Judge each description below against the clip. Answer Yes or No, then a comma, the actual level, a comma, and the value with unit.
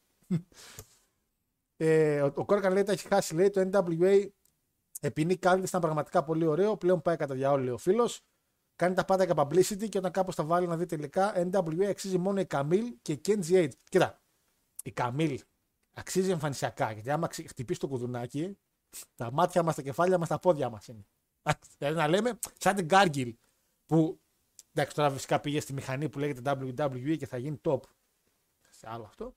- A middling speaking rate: No, fast, 180 wpm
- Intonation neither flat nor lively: Yes, average, 4.6 semitones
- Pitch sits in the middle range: Yes, medium, 165 Hz